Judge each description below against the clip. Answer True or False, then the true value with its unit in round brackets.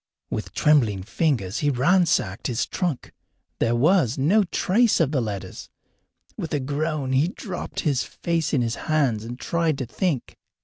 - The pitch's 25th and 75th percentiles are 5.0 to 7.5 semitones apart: True (5.6 semitones)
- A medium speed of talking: True (160 wpm)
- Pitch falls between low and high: True (145 Hz)